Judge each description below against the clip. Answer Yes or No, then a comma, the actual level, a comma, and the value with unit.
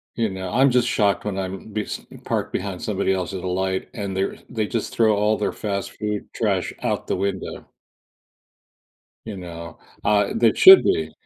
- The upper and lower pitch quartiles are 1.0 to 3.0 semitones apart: Yes, narrow, 2.6 semitones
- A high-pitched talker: No, low, 100 Hz